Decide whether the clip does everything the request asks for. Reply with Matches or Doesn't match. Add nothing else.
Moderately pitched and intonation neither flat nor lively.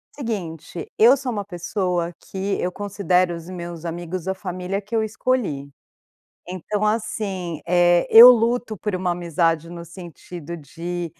Matches